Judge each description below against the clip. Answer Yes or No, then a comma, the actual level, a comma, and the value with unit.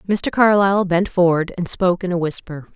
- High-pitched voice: No, medium, 180 Hz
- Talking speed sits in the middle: Yes, average, 195 wpm